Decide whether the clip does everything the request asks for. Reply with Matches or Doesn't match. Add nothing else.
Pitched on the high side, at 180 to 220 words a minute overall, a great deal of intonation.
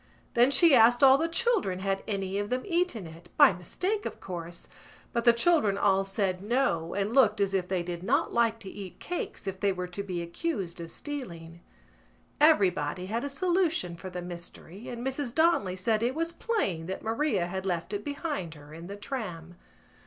Matches